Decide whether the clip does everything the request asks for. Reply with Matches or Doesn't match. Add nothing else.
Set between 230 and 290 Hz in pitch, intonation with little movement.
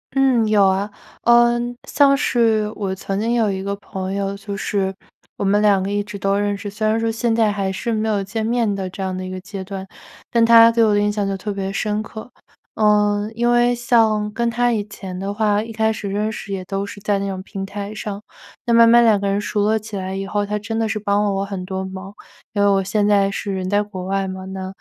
Doesn't match